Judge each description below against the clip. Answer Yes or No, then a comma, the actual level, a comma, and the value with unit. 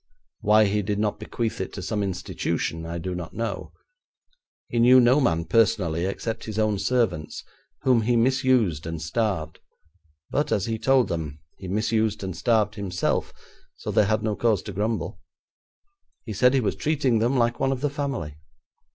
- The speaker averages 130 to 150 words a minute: No, average, 175 wpm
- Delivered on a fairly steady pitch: No, average, 4.1 semitones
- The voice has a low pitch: Yes, low, 110 Hz